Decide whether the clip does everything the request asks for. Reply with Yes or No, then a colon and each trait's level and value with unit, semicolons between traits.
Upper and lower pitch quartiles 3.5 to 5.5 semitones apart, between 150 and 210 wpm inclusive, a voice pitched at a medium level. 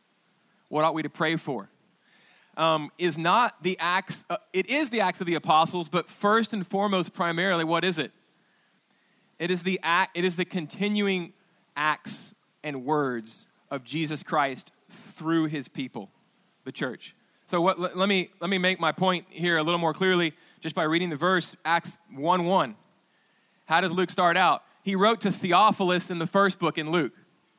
No: average, 2.7 semitones; average, 180 wpm; medium, 180 Hz